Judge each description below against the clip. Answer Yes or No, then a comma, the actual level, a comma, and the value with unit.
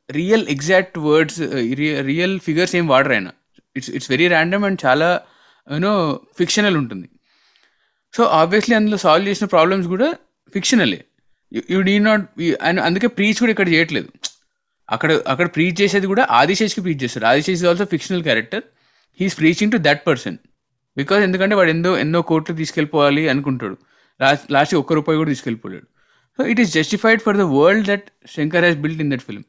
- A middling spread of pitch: Yes, average, 4.8 semitones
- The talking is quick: Yes, fast, 155 wpm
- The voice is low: No, medium, 175 Hz